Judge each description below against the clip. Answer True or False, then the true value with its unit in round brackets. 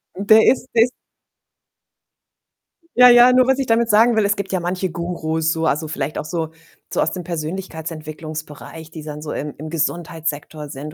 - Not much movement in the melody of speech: False (4.8 semitones)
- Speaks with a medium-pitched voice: True (165 Hz)